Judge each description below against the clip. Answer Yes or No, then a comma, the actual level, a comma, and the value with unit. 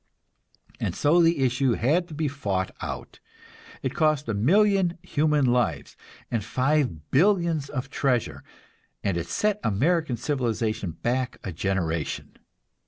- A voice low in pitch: Yes, low, 130 Hz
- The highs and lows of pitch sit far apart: Yes, wide, 6.3 semitones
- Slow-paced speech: Yes, slow, 130 wpm